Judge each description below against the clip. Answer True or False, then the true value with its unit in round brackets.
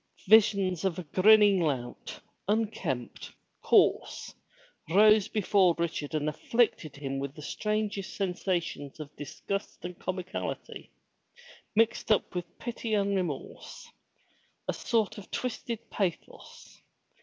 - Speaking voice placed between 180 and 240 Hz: True (190 Hz)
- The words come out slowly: True (115 wpm)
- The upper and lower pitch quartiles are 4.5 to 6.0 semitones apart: True (5.1 semitones)